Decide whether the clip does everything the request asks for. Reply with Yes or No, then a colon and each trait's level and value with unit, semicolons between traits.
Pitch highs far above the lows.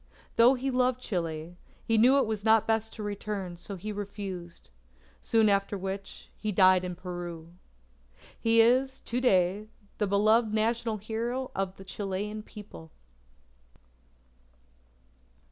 No: average, 3.3 semitones